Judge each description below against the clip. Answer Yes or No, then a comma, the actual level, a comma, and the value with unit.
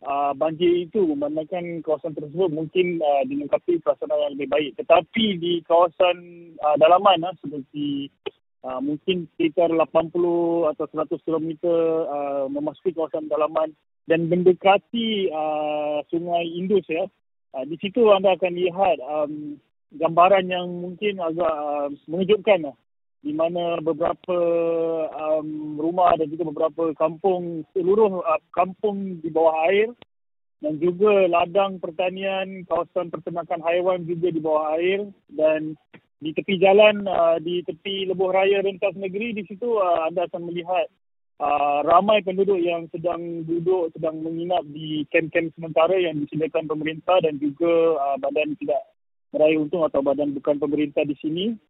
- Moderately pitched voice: Yes, medium, 170 Hz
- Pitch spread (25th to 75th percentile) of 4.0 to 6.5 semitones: No, average, 3.2 semitones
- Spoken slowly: No, average, 140 wpm